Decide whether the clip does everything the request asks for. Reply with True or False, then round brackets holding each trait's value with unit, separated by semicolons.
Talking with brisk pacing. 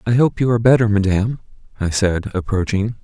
False (180 wpm)